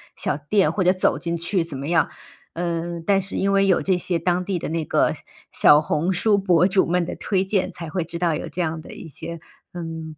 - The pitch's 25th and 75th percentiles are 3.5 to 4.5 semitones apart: No, narrow, 2.4 semitones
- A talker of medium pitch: Yes, medium, 175 Hz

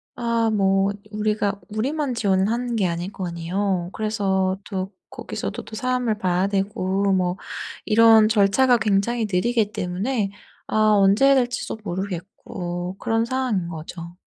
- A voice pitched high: Yes, high, 200 Hz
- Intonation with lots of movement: No, average, 3.3 semitones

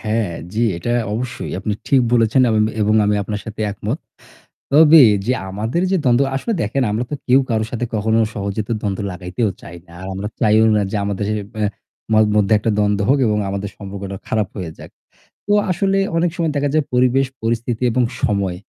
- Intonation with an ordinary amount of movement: Yes, average, 3.7 semitones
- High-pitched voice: No, low, 110 Hz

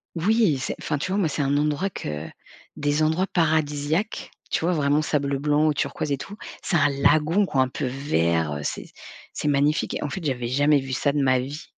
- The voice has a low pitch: No, medium, 145 Hz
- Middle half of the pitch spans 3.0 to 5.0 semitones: No, narrow, 2.5 semitones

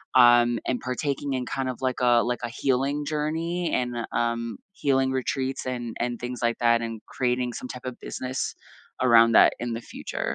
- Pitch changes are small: Yes, narrow, 1.8 semitones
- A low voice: Yes, low, 125 Hz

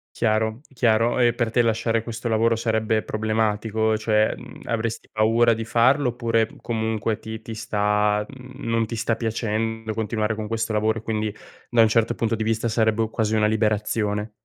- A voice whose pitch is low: Yes, low, 110 Hz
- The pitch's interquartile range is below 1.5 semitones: Yes, narrow, 1.0 semitones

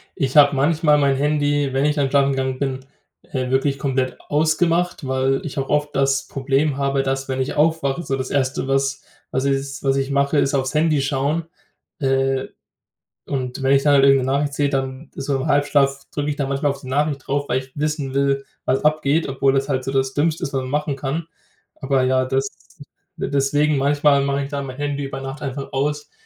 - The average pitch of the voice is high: No, medium, 140 Hz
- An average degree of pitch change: No, narrow, 1.4 semitones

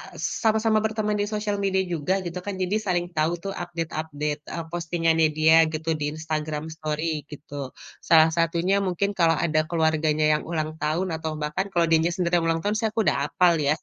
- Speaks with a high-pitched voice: No, medium, 165 Hz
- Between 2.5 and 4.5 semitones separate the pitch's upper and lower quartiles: Yes, average, 2.8 semitones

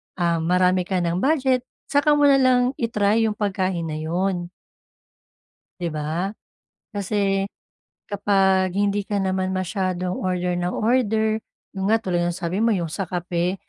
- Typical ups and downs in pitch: Yes, average, 3.0 semitones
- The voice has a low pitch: No, high, 190 Hz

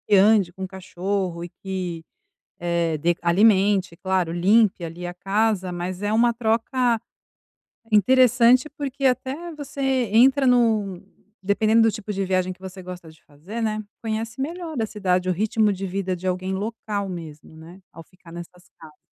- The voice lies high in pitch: Yes, high, 195 Hz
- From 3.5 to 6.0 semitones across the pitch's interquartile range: Yes, average, 3.9 semitones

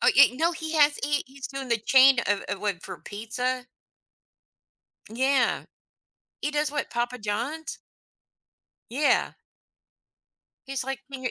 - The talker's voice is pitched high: Yes, very high, 265 Hz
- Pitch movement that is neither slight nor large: Yes, average, 3.4 semitones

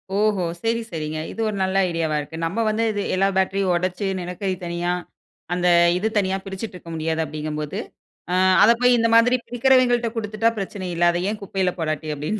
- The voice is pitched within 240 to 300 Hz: No, high, 190 Hz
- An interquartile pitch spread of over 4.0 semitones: Yes, average, 4.4 semitones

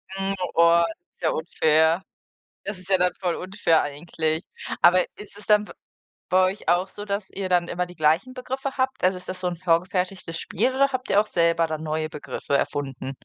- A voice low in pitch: No, medium, 180 Hz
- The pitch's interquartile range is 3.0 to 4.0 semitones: Yes, average, 3.4 semitones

